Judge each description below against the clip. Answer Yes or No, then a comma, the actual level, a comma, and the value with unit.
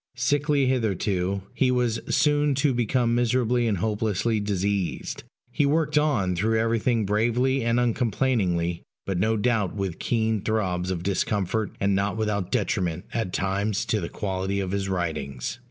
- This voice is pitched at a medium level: No, low, 110 Hz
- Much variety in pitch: No, average, 4.0 semitones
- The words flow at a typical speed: Yes, average, 150 wpm